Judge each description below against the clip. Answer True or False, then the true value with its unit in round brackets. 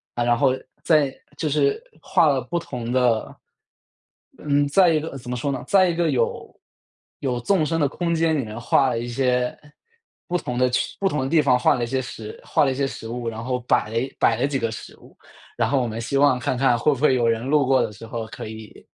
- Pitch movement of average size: True (3.3 semitones)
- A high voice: False (130 Hz)